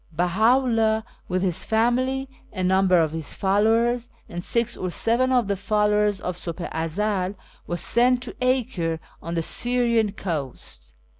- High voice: Yes, high, 210 Hz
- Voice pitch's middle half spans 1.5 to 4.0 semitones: No, average, 5.1 semitones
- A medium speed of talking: Yes, average, 160 wpm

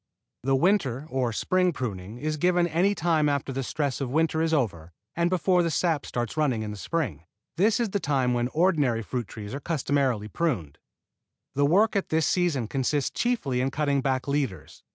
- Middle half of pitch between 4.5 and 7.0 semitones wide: Yes, average, 5.3 semitones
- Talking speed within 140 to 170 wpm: No, average, 195 wpm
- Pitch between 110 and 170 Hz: Yes, medium, 140 Hz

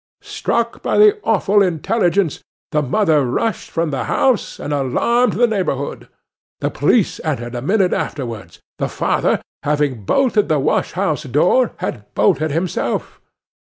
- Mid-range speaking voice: Yes, medium, 160 Hz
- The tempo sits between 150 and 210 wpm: No, average, 140 wpm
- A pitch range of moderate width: No, wide, 7.6 semitones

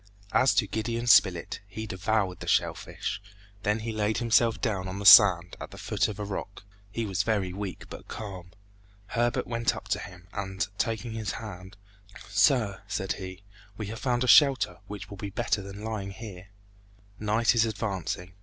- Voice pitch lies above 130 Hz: No, low, 105 Hz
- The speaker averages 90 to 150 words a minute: No, average, 180 wpm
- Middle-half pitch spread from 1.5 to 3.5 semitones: Yes, average, 2.9 semitones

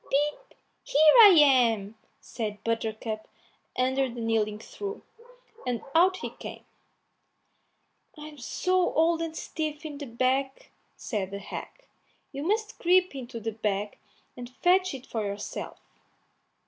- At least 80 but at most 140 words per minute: Yes, slow, 135 wpm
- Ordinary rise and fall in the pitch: No, wide, 6.3 semitones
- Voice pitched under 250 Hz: No, very high, 265 Hz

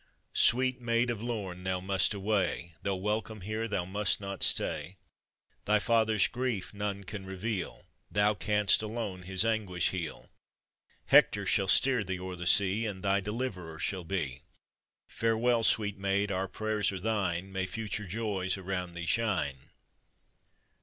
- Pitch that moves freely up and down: No, average, 2.8 semitones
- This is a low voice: Yes, low, 100 Hz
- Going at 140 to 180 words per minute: Yes, average, 145 wpm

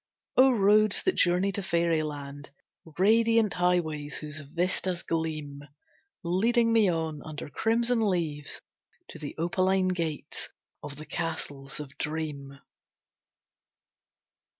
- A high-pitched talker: No, medium, 170 Hz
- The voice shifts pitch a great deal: No, average, 4.5 semitones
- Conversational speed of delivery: No, slow, 105 wpm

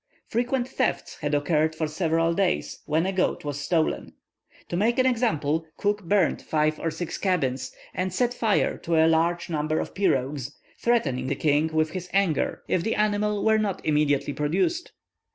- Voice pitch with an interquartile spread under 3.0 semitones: No, average, 5.2 semitones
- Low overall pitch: No, medium, 165 Hz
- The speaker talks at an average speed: Yes, average, 170 wpm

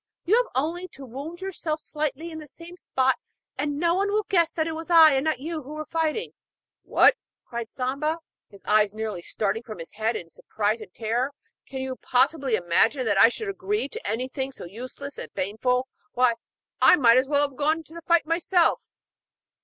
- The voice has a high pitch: Yes, very high, 275 Hz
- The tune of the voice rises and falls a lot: Yes, wide, 5.7 semitones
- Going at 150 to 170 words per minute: No, average, 200 wpm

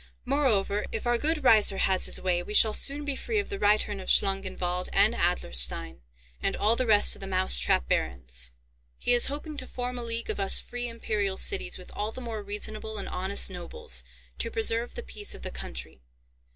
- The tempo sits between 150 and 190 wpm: No, fast, 205 wpm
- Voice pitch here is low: No, high, 215 Hz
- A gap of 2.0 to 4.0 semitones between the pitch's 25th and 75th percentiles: No, average, 4.7 semitones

